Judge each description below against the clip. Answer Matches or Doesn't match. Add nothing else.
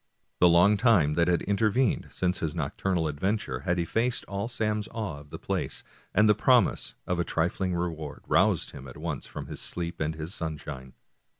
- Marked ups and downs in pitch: Doesn't match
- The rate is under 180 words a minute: Doesn't match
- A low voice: Matches